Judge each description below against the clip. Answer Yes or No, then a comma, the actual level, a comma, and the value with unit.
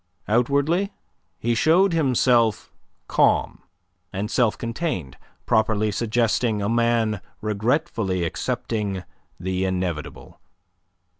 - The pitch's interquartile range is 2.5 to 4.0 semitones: Yes, average, 3.7 semitones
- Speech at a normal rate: No, slow, 85 wpm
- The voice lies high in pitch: No, low, 115 Hz